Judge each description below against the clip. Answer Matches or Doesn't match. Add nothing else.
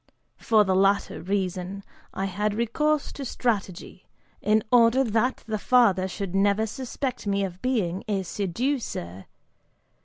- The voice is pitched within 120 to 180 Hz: Doesn't match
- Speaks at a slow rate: Matches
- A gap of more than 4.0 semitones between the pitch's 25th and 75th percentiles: Doesn't match